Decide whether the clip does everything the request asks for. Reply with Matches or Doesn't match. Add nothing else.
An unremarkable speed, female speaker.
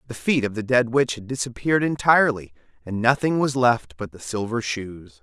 Doesn't match